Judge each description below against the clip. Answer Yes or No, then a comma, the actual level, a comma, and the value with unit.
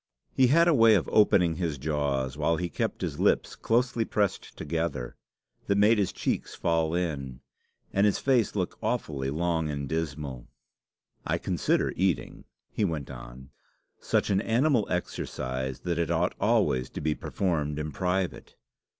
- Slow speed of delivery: No, average, 155 wpm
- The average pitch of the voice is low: Yes, very low, 80 Hz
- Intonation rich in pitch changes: Yes, wide, 6.0 semitones